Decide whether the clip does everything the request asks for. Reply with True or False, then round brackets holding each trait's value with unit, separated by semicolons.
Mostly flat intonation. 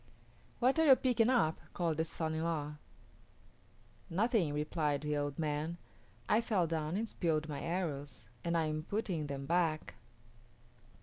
False (3.3 semitones)